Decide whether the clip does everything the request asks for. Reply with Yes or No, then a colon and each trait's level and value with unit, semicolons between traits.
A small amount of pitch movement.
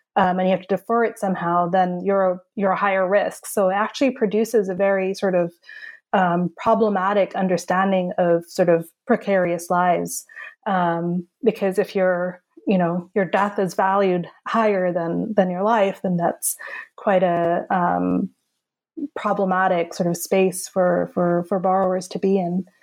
Yes: narrow, 2.3 semitones